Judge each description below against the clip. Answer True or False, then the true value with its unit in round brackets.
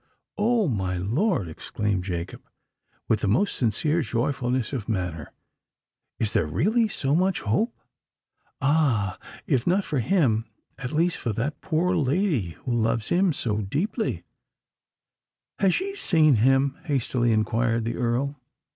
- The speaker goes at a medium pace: False (130 wpm)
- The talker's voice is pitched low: True (130 Hz)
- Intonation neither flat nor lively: False (7.4 semitones)